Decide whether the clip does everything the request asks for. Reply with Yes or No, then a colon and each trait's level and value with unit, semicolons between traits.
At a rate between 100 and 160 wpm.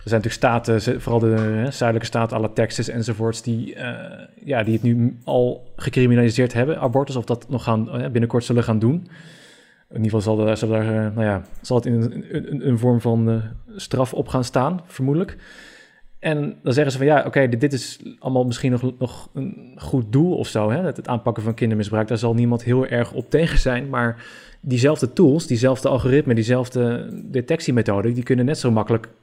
No: fast, 200 wpm